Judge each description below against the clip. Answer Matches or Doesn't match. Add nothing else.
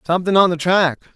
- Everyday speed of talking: Doesn't match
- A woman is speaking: Doesn't match